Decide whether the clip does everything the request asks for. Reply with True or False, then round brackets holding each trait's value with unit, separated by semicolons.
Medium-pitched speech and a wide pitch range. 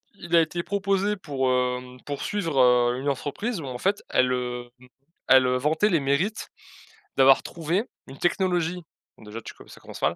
True (145 Hz; 6.1 semitones)